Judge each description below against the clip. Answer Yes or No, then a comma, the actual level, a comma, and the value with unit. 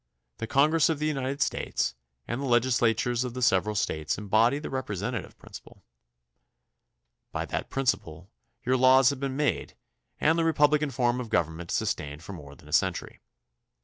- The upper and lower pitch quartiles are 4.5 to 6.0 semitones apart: Yes, average, 4.9 semitones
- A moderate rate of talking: Yes, average, 165 wpm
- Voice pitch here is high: No, low, 125 Hz